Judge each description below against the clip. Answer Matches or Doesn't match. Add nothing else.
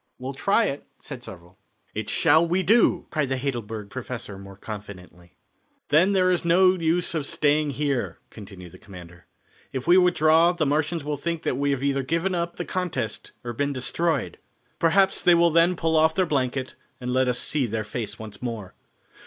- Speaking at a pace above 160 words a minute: Matches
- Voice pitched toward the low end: Doesn't match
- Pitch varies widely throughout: Matches